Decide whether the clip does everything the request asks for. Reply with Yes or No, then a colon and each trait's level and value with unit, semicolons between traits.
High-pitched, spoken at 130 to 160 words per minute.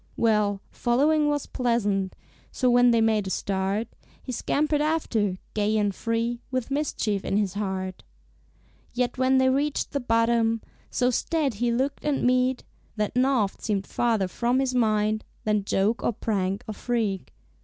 Yes: high, 230 Hz; average, 155 wpm